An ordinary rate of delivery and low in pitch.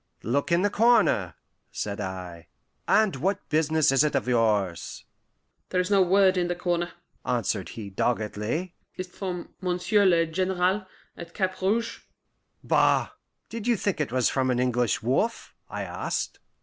No: average, 150 wpm; medium, 170 Hz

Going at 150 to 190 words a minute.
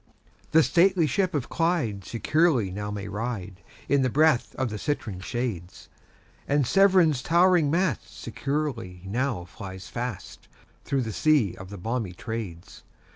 No: average, 140 wpm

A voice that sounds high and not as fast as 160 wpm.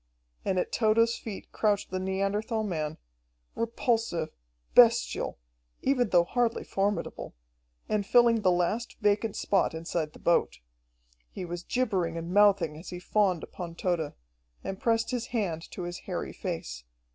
Yes: high, 195 Hz; average, 145 wpm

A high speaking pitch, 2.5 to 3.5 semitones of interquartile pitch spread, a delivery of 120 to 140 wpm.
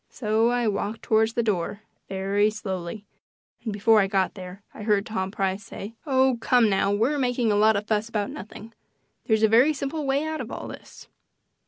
No: high, 215 Hz; average, 2.8 semitones; average, 195 wpm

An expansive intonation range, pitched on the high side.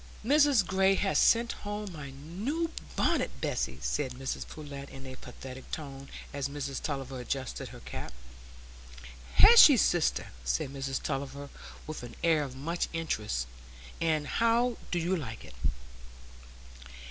No: wide, 6.2 semitones; medium, 145 Hz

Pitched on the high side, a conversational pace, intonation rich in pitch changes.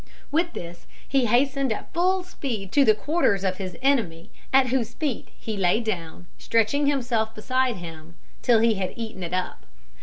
Yes: high, 225 Hz; average, 180 wpm; wide, 6.4 semitones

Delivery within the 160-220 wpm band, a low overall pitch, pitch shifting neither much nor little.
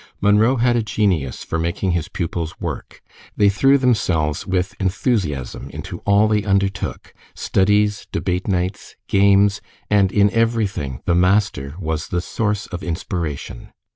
No: average, 140 wpm; very low, 95 Hz; average, 3.4 semitones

